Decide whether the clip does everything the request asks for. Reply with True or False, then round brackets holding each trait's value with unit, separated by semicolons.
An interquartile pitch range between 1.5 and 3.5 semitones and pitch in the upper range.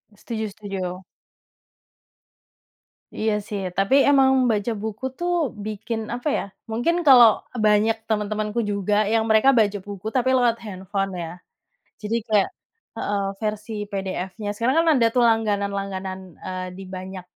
True (2.6 semitones; 210 Hz)